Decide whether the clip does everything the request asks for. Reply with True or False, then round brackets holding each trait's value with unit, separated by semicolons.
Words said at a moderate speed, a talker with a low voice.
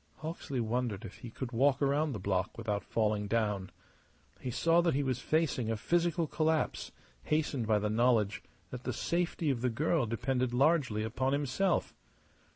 True (165 wpm; 125 Hz)